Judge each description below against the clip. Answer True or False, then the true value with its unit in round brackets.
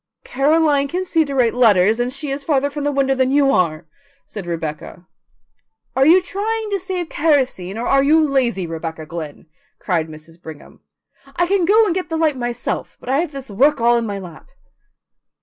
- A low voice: False (270 Hz)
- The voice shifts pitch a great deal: True (8.6 semitones)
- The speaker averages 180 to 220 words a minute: True (195 wpm)